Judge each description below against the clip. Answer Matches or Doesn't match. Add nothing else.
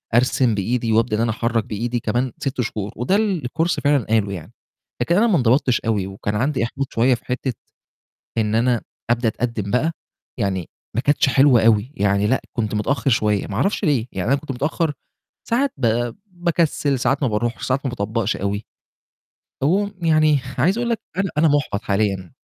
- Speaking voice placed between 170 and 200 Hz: Doesn't match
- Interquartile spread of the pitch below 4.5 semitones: Doesn't match